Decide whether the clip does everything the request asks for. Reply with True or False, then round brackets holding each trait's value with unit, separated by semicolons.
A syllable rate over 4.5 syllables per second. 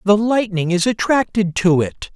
False (4.4 syllables/s)